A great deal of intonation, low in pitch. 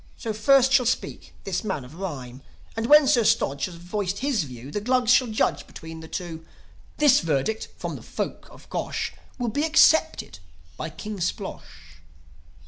No: wide, 7.7 semitones; high, 205 Hz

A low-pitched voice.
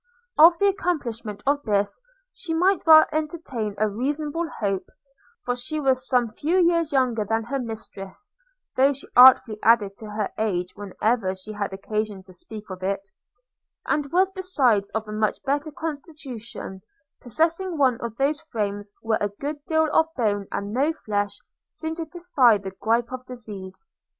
No: high, 240 Hz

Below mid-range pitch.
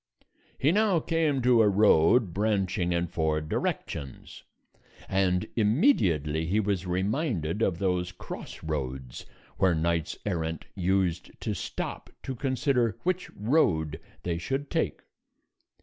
Yes: very low, 95 Hz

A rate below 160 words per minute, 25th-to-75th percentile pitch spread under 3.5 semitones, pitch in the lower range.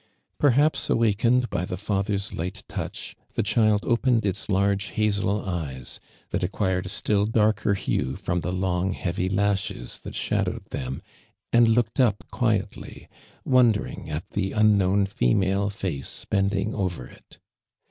Yes: average, 140 wpm; average, 2.8 semitones; low, 100 Hz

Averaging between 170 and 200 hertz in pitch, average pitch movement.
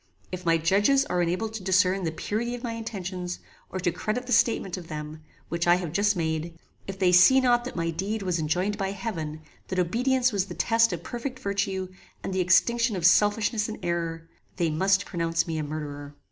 Yes: medium, 185 Hz; average, 4.6 semitones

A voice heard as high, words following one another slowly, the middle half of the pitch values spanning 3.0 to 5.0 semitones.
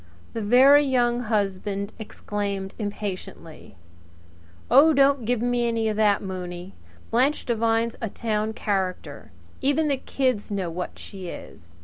Yes: high, 220 Hz; slow, 130 wpm; average, 3.7 semitones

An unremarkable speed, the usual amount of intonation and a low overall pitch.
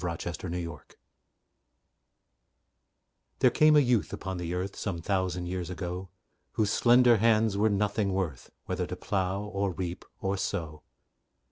Yes: average, 150 wpm; average, 3.0 semitones; very low, 95 Hz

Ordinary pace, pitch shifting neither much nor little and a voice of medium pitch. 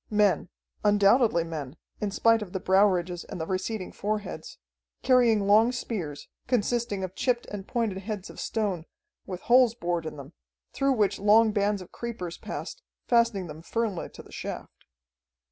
No: average, 160 wpm; average, 4.0 semitones; high, 205 Hz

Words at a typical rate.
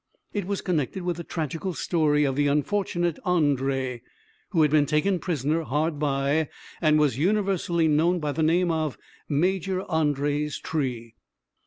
Yes: average, 150 wpm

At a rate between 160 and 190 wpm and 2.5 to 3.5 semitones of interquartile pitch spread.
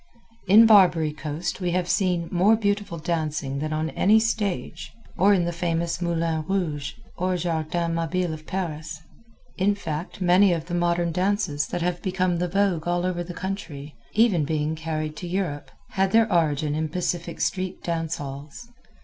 Yes: average, 165 wpm; average, 2.9 semitones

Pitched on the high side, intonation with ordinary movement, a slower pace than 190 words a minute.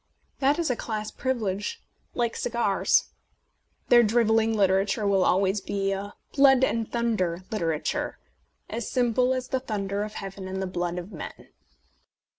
Yes: high, 215 Hz; average, 3.6 semitones; average, 150 wpm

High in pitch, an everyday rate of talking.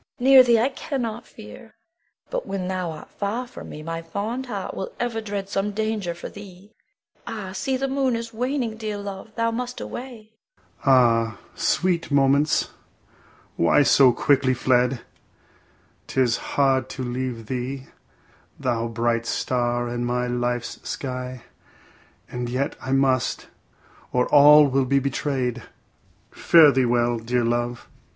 No: medium, 140 Hz; average, 145 wpm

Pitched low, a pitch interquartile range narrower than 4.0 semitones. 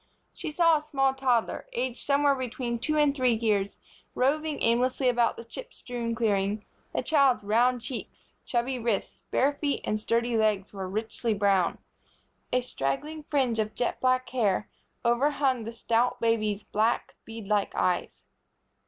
No: high, 240 Hz; average, 3.5 semitones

